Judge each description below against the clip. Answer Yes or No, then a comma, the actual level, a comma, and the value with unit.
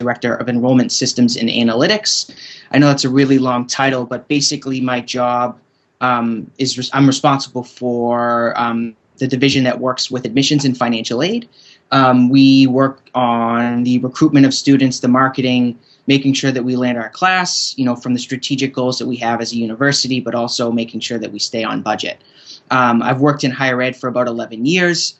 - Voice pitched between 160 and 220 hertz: No, low, 125 Hz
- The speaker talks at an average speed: Yes, average, 195 wpm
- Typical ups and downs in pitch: No, narrow, 1.9 semitones